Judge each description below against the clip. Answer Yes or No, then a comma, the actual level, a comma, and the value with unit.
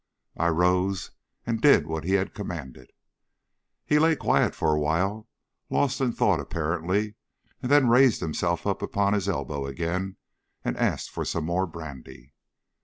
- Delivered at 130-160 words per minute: Yes, average, 155 wpm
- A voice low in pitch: Yes, very low, 90 Hz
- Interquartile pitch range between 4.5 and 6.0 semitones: Yes, average, 4.9 semitones